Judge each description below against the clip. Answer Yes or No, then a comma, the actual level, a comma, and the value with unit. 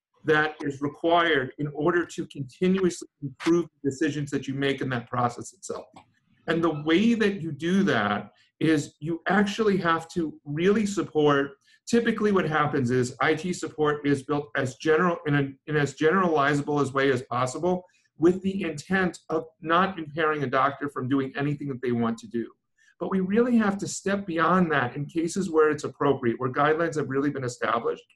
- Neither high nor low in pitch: Yes, medium, 155 Hz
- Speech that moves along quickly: No, average, 180 wpm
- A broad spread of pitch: No, average, 3.8 semitones